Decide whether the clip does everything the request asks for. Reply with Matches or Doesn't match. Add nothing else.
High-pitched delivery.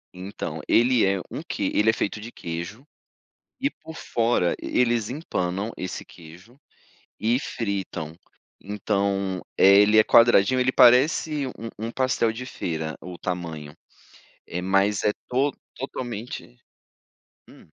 Doesn't match